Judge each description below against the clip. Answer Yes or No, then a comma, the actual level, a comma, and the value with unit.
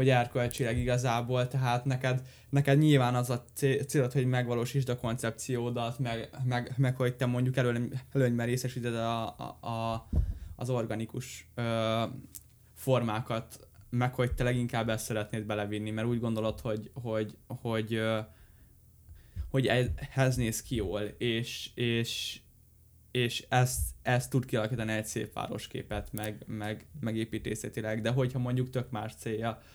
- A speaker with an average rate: Yes, average, 140 wpm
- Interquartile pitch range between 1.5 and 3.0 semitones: Yes, narrow, 2.5 semitones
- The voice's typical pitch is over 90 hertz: Yes, low, 120 Hz